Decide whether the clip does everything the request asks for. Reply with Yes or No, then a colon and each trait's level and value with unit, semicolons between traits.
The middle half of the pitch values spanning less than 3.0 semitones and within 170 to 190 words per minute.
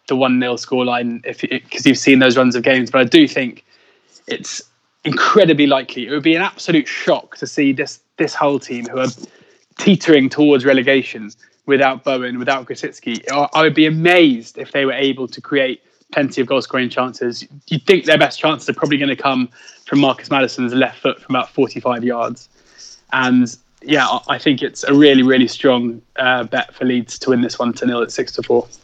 No: narrow, 2.6 semitones; average, 200 wpm